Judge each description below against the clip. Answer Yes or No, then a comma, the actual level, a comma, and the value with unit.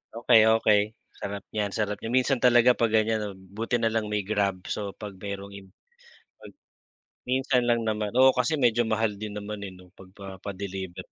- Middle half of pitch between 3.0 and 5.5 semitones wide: No, narrow, 2.6 semitones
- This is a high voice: No, low, 105 Hz